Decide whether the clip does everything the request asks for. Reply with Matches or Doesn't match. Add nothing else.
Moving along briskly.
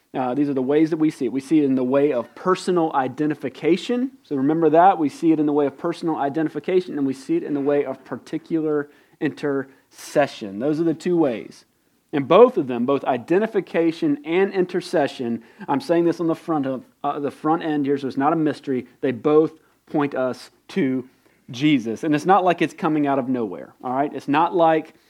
Matches